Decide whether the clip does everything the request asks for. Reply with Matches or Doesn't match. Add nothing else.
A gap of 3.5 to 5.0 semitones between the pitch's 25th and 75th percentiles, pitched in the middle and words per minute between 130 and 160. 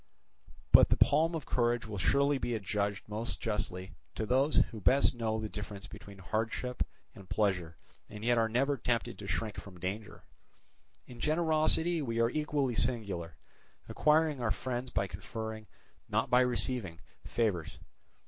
Doesn't match